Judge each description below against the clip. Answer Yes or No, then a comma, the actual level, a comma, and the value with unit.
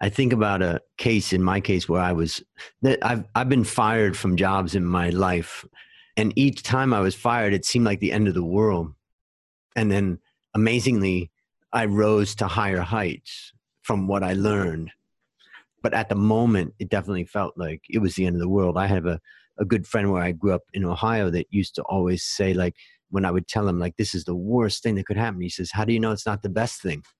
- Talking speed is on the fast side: Yes, fast, 230 wpm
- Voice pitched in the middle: No, low, 100 Hz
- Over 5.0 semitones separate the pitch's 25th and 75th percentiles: No, average, 3.2 semitones